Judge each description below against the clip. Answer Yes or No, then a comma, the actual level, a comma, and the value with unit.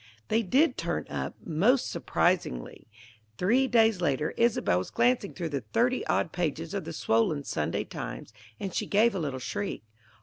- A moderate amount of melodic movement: No, wide, 7.5 semitones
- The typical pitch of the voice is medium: Yes, medium, 180 Hz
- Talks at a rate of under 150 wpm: No, average, 165 wpm